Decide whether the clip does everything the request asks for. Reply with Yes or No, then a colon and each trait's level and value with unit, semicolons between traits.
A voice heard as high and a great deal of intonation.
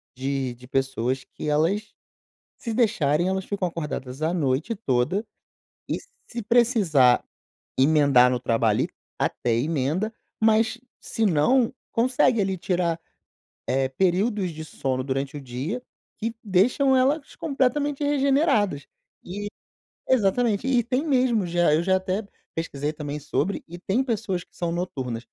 No: medium, 180 Hz; wide, 8.4 semitones